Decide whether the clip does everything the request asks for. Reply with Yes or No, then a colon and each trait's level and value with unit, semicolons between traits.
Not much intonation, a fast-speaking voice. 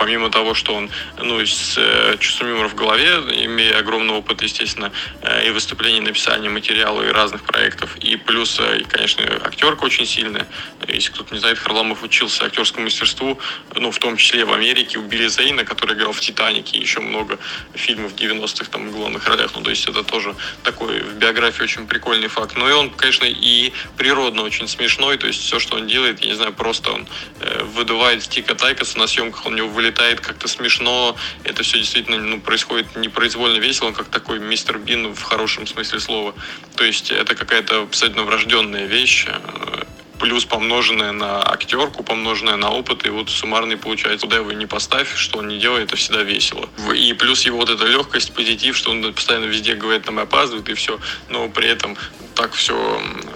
Yes: narrow, 1.3 semitones; fast, 190 wpm